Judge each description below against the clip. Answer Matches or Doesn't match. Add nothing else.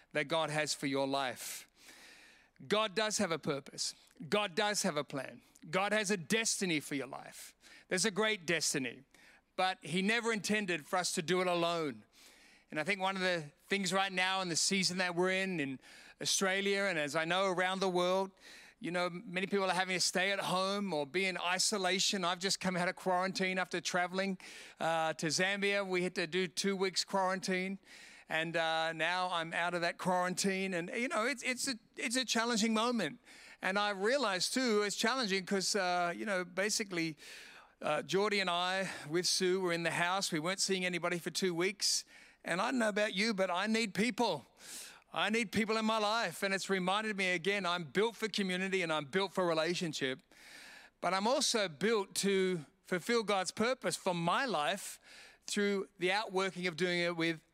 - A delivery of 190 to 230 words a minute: Matches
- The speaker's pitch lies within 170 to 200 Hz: Matches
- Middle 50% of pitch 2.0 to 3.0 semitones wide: Matches